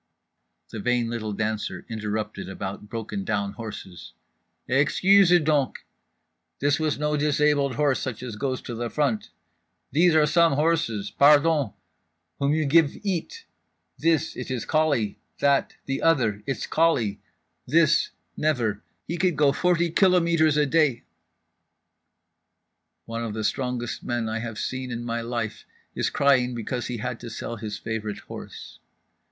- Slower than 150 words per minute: Yes, slow, 135 wpm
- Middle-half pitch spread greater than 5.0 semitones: Yes, wide, 5.4 semitones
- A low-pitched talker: Yes, low, 130 Hz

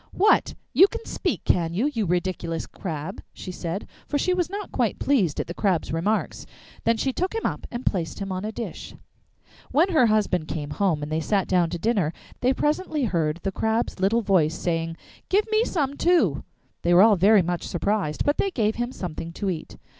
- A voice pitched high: Yes, high, 200 Hz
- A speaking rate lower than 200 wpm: No, fast, 205 wpm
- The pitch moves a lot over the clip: Yes, wide, 7.3 semitones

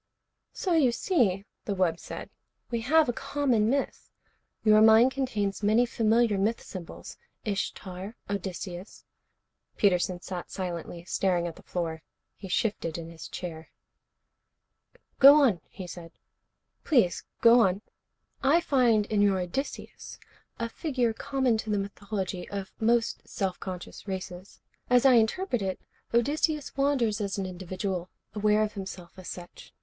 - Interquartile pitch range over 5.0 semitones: No, average, 4.5 semitones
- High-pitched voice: Yes, high, 205 Hz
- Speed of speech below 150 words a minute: Yes, average, 140 wpm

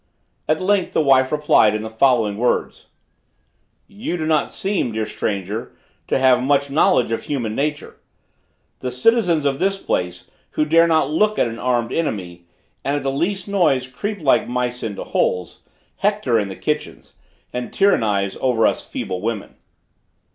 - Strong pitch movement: Yes, wide, 6.2 semitones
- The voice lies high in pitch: No, low, 130 Hz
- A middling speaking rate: Yes, average, 160 wpm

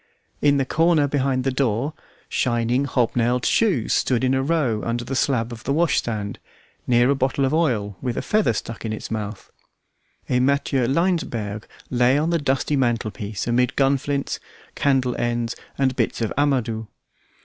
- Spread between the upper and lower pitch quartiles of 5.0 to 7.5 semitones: No, average, 3.2 semitones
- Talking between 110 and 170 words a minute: Yes, average, 165 wpm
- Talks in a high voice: No, low, 130 Hz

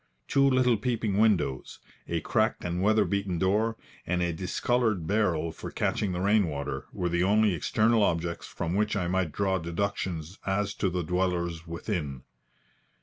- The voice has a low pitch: Yes, very low, 95 Hz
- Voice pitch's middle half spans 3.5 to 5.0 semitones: Yes, average, 3.8 semitones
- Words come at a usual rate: Yes, average, 160 wpm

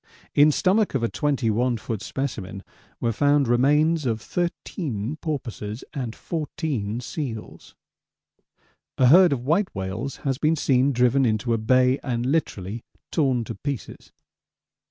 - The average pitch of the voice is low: Yes, low, 130 Hz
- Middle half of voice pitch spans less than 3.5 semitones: No, average, 4.3 semitones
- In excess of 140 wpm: No, slow, 135 wpm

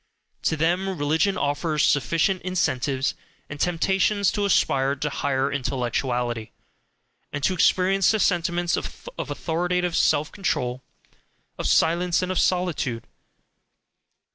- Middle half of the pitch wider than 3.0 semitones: Yes, average, 4.7 semitones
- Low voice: No, medium, 165 Hz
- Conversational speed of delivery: No, slow, 115 wpm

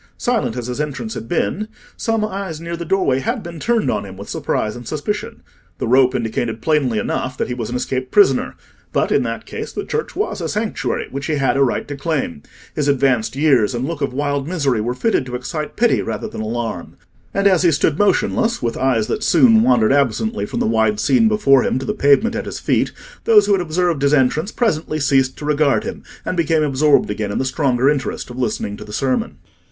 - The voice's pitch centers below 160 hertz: Yes, medium, 140 Hz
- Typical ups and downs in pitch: No, wide, 6.0 semitones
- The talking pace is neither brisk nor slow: No, fast, 220 wpm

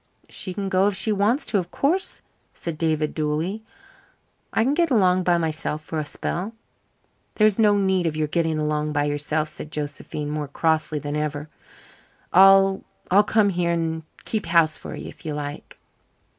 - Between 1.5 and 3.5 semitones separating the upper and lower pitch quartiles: No, average, 4.3 semitones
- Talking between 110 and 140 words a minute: No, average, 175 wpm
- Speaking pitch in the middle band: Yes, medium, 170 Hz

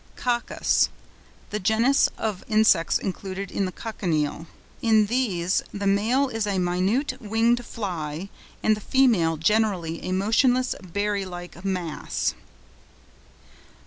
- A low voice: No, high, 200 Hz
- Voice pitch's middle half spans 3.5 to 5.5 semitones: Yes, average, 3.8 semitones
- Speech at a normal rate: No, slow, 110 wpm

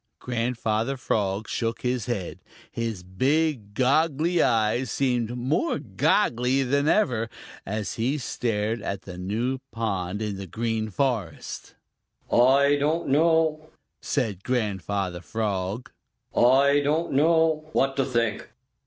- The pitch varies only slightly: No, average, 4.7 semitones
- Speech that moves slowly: Yes, slow, 120 wpm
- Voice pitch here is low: Yes, low, 120 Hz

